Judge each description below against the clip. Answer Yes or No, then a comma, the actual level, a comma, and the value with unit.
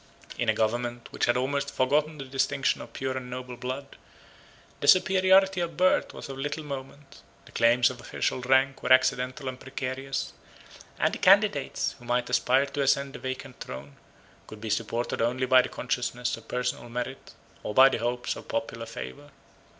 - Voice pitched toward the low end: Yes, low, 130 Hz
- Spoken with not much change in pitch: Yes, narrow, 2.2 semitones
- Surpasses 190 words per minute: No, average, 180 wpm